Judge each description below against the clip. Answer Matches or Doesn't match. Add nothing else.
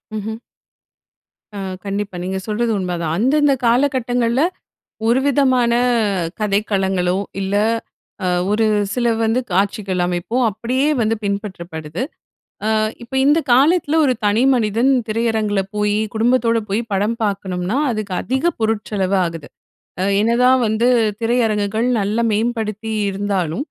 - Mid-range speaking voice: Doesn't match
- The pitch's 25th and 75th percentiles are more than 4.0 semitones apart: Doesn't match